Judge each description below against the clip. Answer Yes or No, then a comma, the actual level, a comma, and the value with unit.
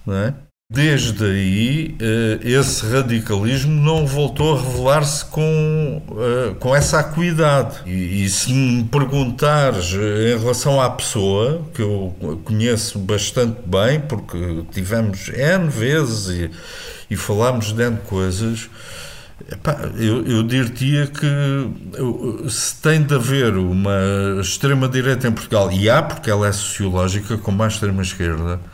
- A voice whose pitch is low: Yes, low, 120 Hz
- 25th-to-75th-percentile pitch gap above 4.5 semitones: Yes, wide, 5.5 semitones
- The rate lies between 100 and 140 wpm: Yes, average, 125 wpm